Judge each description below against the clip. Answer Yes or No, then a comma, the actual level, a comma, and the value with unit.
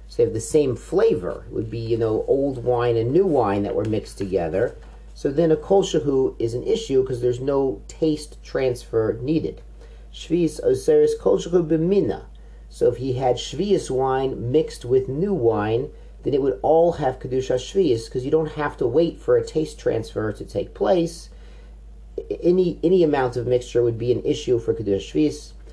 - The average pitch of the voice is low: Yes, low, 130 Hz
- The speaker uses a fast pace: No, average, 180 wpm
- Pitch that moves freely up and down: Yes, wide, 6.3 semitones